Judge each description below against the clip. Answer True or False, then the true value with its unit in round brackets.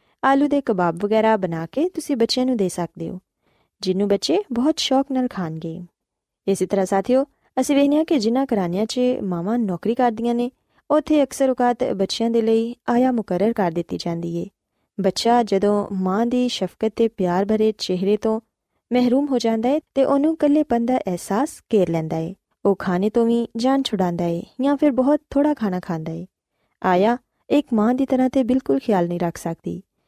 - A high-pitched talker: True (225 Hz)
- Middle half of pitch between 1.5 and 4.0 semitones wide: False (5.5 semitones)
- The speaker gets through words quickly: True (180 wpm)